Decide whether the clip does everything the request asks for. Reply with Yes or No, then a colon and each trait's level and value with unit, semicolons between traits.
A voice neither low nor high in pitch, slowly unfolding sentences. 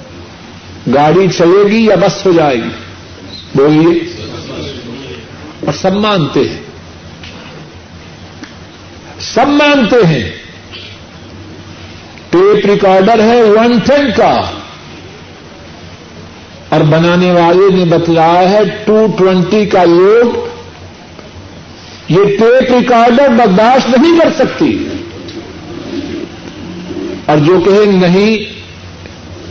Yes: medium, 175 Hz; slow, 85 wpm